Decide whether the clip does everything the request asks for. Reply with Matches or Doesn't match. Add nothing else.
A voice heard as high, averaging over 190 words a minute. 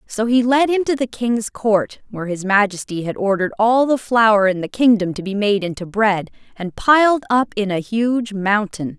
Matches